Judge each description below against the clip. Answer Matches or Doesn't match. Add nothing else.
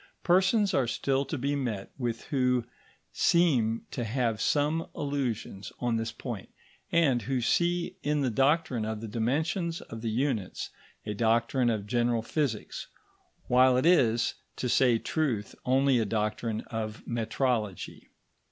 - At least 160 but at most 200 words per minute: Doesn't match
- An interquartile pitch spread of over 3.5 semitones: Matches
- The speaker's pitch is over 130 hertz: Doesn't match